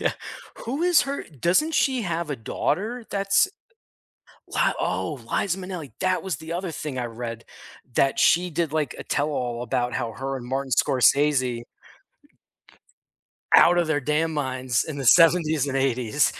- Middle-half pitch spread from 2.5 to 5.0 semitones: No, wide, 5.6 semitones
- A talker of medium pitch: Yes, medium, 150 Hz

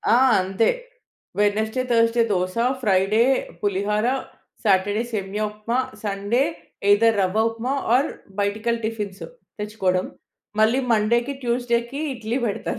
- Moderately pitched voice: No, high, 215 Hz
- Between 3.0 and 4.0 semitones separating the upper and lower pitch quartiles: No, narrow, 2.6 semitones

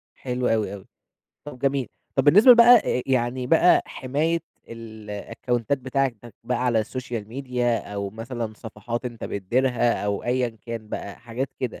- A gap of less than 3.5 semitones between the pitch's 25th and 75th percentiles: Yes, narrow, 2.6 semitones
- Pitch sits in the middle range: No, low, 120 Hz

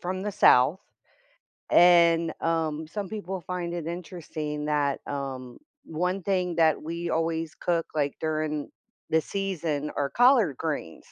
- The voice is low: No, medium, 165 Hz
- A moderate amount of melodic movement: Yes, average, 3.0 semitones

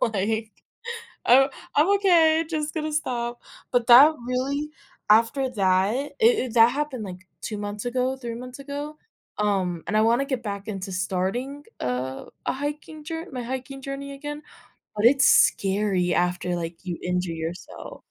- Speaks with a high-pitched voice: Yes, high, 240 Hz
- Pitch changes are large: Yes, wide, 6.4 semitones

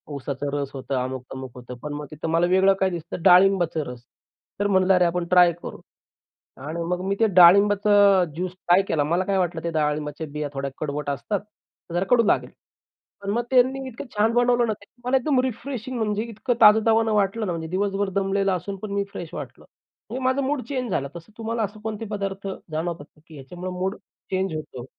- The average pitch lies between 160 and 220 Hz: Yes, high, 190 Hz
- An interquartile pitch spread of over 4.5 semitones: Yes, average, 5.2 semitones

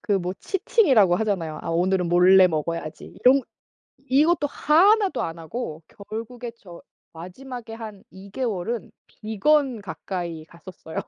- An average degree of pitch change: No, wide, 6.5 semitones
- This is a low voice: No, high, 205 Hz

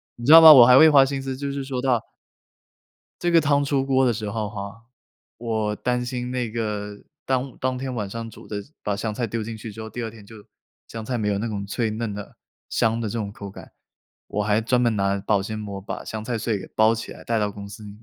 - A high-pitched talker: No, low, 115 Hz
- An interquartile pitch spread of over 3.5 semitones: No, average, 3.2 semitones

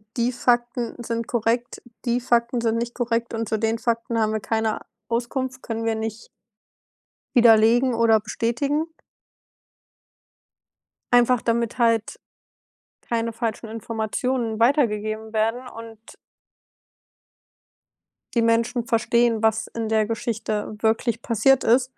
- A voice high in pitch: Yes, high, 230 Hz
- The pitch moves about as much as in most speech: No, narrow, 1.3 semitones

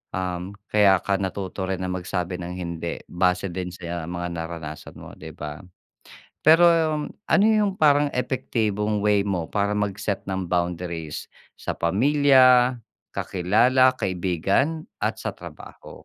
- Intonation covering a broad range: Yes, wide, 5.8 semitones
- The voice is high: No, very low, 95 Hz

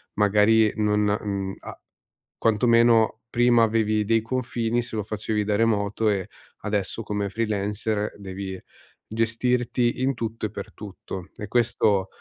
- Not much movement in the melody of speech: Yes, narrow, 1.9 semitones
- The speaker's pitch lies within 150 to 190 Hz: No, low, 110 Hz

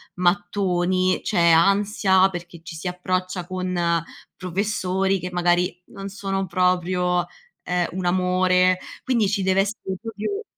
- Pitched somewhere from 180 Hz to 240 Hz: Yes, medium, 185 Hz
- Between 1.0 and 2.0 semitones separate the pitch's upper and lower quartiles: Yes, narrow, 1.5 semitones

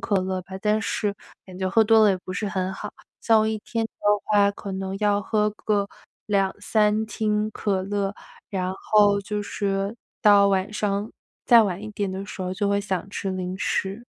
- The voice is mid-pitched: No, high, 200 Hz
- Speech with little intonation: Yes, narrow, 1.7 semitones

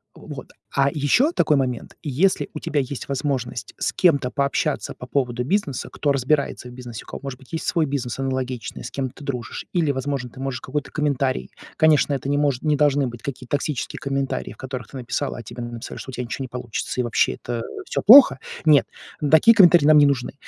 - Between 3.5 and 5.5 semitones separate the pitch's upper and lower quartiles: No, average, 2.7 semitones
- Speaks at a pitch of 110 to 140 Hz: Yes, low, 135 Hz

